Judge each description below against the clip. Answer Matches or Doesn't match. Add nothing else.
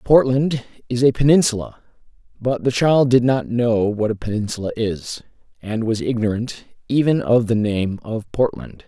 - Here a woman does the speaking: Doesn't match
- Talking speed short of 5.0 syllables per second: Matches